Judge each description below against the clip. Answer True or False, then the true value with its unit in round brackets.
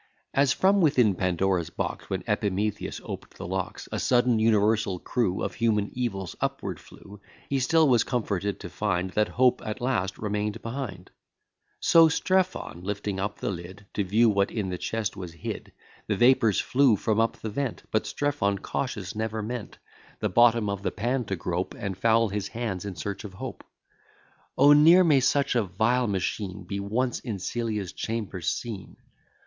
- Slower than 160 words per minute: False (175 wpm)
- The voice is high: False (105 Hz)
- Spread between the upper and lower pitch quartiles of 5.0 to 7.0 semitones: False (3.9 semitones)